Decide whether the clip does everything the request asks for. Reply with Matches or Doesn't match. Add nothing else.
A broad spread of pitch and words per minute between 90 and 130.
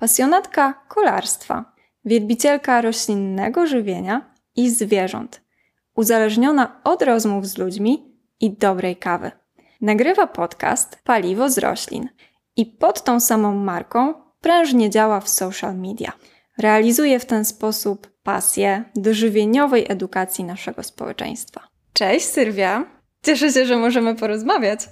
Doesn't match